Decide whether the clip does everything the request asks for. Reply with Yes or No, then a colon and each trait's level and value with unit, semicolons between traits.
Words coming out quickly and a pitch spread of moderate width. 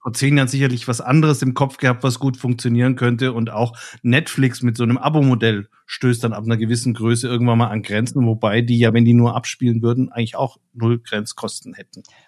No: fast, 210 wpm; narrow, 1.8 semitones